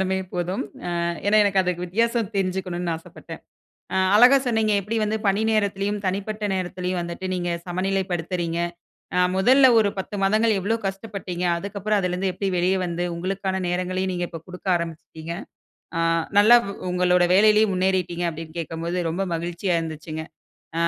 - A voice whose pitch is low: No, medium, 185 Hz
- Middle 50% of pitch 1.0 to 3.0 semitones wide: Yes, narrow, 2.5 semitones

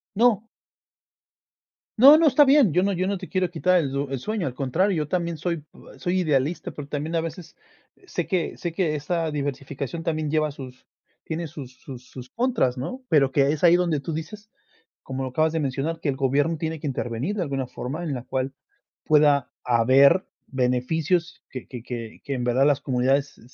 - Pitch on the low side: No, medium, 150 Hz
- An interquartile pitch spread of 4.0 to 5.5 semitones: Yes, average, 4.5 semitones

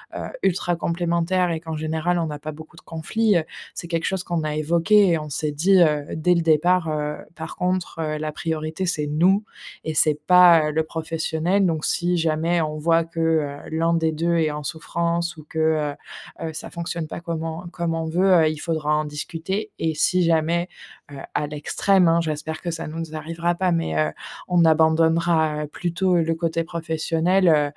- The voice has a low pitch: No, medium, 165 Hz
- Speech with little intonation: Yes, narrow, 1.7 semitones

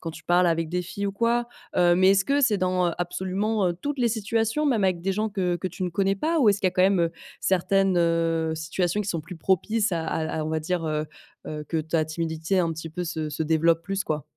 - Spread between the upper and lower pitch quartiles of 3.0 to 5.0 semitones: Yes, average, 3.3 semitones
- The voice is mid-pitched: Yes, medium, 180 Hz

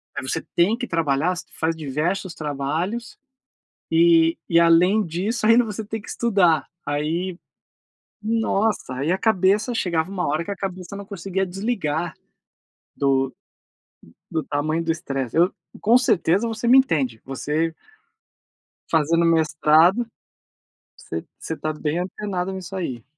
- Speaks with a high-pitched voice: No, medium, 170 Hz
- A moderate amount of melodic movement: Yes, average, 4.3 semitones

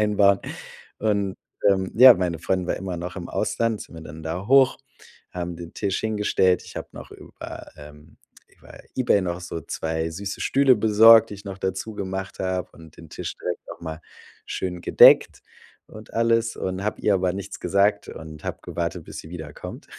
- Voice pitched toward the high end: No, very low, 95 Hz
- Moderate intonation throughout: Yes, average, 3.5 semitones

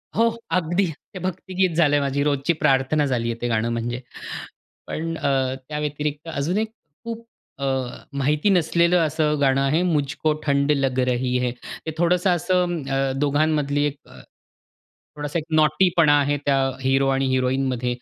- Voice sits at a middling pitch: Yes, medium, 145 Hz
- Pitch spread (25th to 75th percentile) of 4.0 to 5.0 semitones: No, average, 3.6 semitones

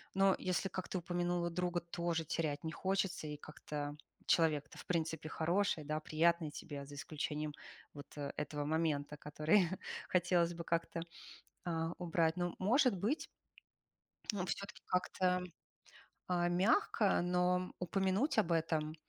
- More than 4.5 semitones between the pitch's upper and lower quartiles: No, average, 2.7 semitones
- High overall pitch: No, medium, 170 Hz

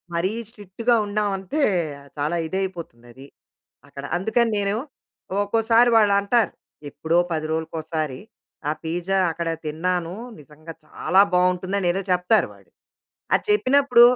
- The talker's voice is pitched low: No, medium, 185 Hz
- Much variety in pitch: No, average, 4.4 semitones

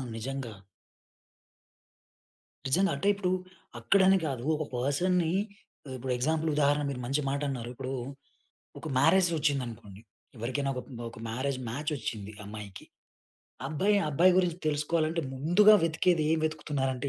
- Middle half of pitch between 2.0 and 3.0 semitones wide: No, average, 4.4 semitones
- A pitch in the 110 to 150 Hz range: Yes, medium, 140 Hz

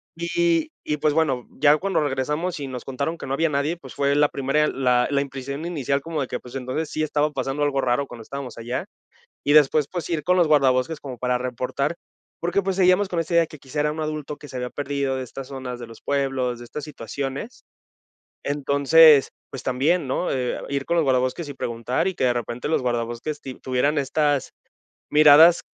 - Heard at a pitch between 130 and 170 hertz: Yes, medium, 140 Hz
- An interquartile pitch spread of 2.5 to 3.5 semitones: Yes, average, 3.1 semitones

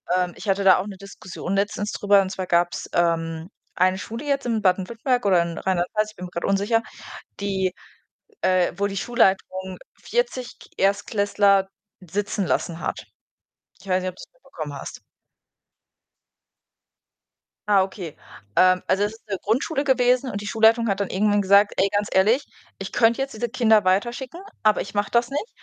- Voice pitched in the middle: No, high, 200 Hz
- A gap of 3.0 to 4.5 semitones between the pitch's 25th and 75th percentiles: Yes, average, 3.3 semitones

